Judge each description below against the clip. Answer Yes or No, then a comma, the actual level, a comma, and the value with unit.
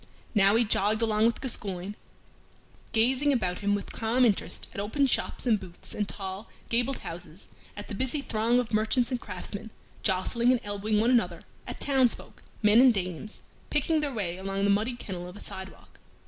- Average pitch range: Yes, average, 3.7 semitones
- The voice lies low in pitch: No, high, 215 Hz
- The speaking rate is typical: Yes, average, 180 wpm